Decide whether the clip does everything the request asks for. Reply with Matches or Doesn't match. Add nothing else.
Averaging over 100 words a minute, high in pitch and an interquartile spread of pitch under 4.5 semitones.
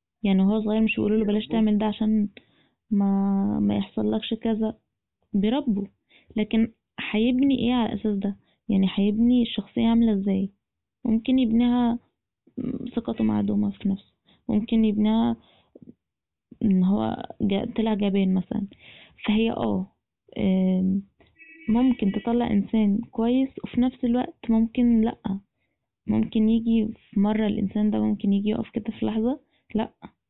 Matches